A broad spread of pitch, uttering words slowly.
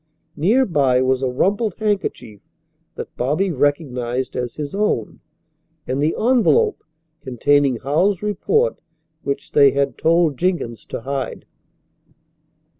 Yes: wide, 7.1 semitones; slow, 115 wpm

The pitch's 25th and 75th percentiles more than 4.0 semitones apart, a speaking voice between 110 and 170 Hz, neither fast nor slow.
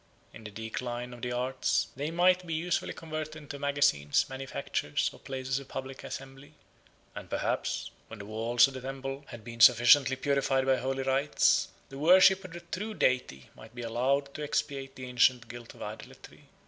No: average, 3.0 semitones; low, 135 Hz; average, 180 wpm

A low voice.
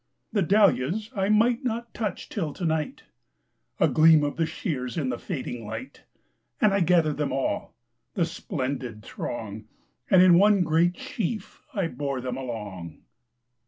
No: medium, 160 Hz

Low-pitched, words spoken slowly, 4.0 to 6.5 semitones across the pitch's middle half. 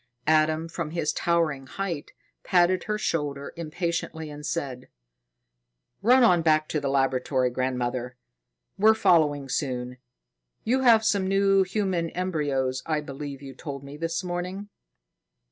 No: medium, 155 Hz; slow, 130 wpm; average, 4.7 semitones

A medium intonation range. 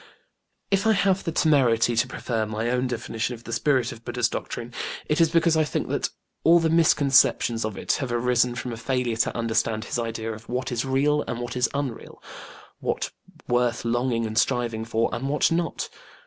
Yes: average, 3.5 semitones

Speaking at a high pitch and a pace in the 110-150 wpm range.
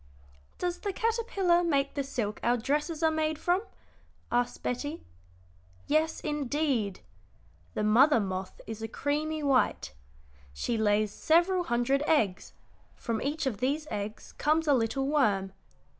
Yes: very high, 280 Hz; slow, 135 wpm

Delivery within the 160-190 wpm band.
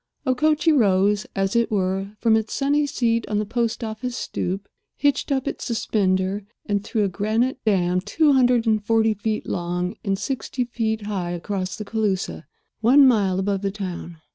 Yes: average, 170 wpm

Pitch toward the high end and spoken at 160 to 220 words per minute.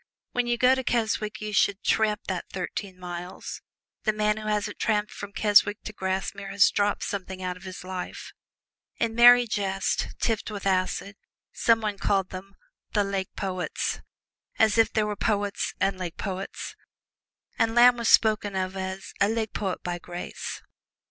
Yes: high, 205 Hz; average, 170 wpm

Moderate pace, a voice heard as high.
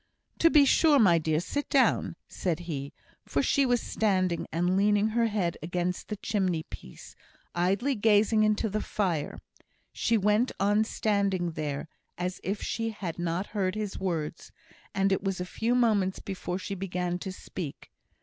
Yes: average, 165 wpm; high, 195 Hz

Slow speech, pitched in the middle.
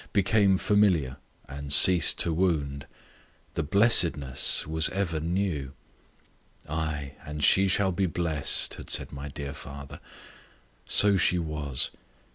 No: slow, 120 wpm; very low, 80 Hz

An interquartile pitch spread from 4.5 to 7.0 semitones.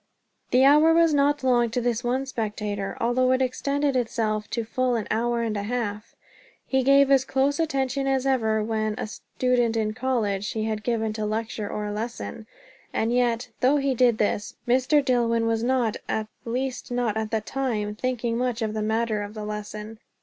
No: average, 3.1 semitones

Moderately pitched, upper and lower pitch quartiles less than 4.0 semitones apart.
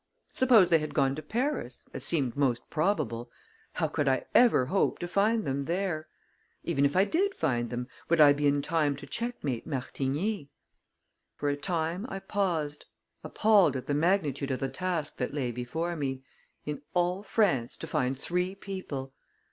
No: medium, 150 Hz; wide, 5.6 semitones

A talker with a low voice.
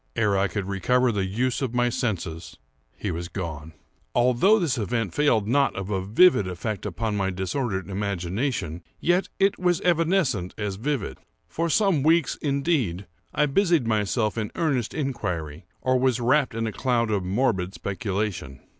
Yes: low, 115 Hz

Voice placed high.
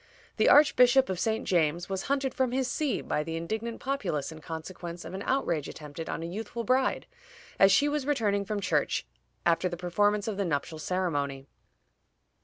Yes: high, 195 Hz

